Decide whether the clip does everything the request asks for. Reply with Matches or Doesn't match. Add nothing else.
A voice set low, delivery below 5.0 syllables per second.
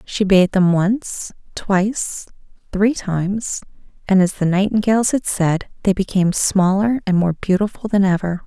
Doesn't match